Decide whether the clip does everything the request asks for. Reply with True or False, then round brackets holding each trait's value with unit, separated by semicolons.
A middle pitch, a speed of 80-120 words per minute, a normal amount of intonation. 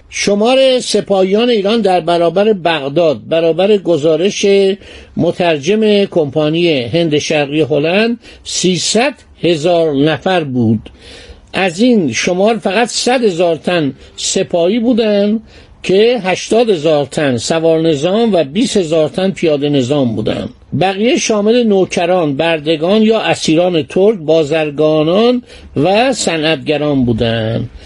True (175 Hz; 110 wpm; 4.8 semitones)